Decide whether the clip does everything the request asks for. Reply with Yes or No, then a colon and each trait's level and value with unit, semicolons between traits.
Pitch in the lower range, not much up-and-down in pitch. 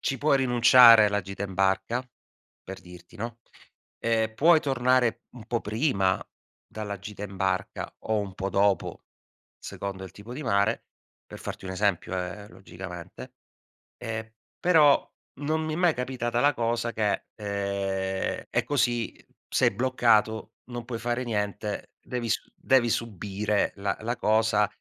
No: low, 110 Hz; average, 3.5 semitones